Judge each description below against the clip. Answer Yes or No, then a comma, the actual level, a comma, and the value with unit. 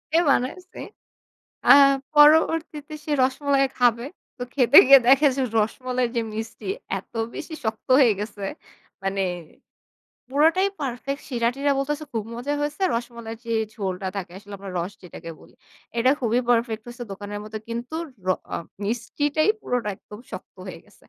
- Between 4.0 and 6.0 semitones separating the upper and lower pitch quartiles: Yes, average, 4.5 semitones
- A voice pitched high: Yes, high, 245 Hz